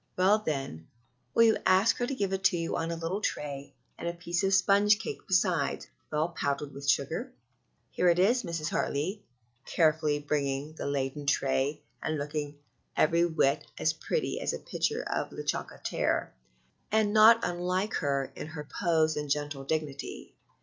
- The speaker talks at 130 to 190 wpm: Yes, average, 170 wpm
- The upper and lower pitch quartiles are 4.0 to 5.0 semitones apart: Yes, average, 4.6 semitones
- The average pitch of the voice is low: No, medium, 160 Hz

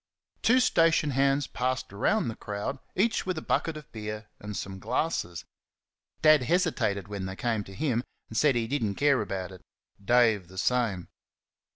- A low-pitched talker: Yes, low, 120 Hz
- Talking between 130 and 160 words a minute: No, average, 175 wpm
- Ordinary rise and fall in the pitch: No, wide, 6.3 semitones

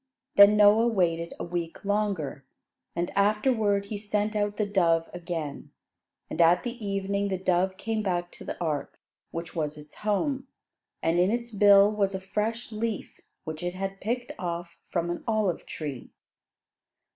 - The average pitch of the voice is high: Yes, high, 195 Hz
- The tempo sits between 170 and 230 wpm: No, average, 160 wpm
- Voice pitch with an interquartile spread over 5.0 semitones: No, average, 3.5 semitones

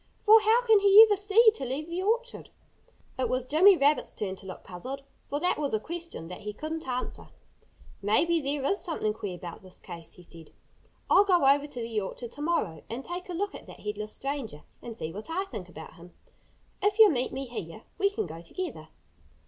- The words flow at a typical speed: No, fast, 215 wpm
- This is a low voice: No, very high, 275 Hz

